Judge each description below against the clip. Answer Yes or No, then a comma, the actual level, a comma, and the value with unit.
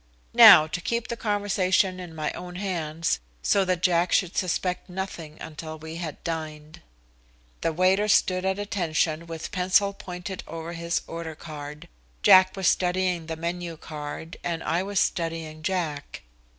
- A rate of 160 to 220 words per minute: No, average, 150 wpm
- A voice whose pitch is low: No, medium, 170 Hz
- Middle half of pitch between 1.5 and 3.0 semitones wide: Yes, narrow, 2.6 semitones